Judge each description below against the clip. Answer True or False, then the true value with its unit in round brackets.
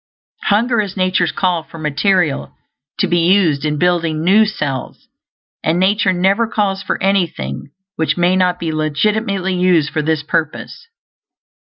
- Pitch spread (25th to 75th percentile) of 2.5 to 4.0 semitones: True (3.7 semitones)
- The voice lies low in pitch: False (180 Hz)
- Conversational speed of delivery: True (145 wpm)